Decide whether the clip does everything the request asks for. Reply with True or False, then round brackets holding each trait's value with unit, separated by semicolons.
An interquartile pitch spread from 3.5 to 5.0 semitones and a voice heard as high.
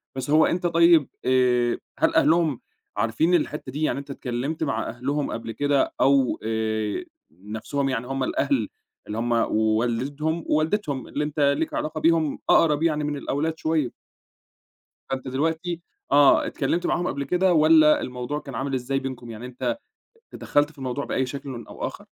False (4.0 semitones; 140 Hz)